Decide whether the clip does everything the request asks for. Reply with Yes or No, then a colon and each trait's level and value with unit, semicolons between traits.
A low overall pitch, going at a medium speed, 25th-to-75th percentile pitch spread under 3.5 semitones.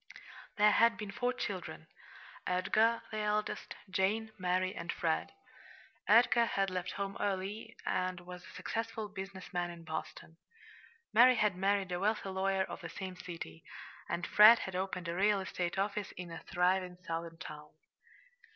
No: high, 190 Hz; average, 155 wpm; average, 2.8 semitones